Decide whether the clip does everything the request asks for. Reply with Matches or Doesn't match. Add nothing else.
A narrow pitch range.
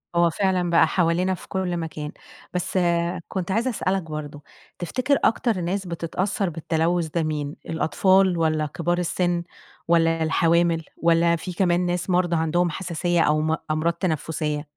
Matches